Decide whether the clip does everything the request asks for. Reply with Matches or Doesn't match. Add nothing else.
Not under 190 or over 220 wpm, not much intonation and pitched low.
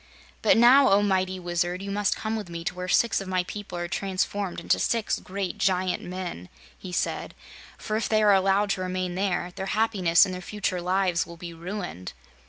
Doesn't match